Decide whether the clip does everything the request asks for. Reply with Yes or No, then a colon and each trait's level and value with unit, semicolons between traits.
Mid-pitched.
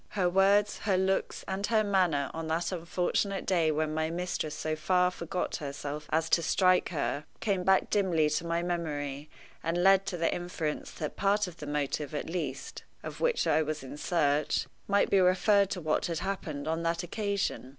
Yes: medium, 170 Hz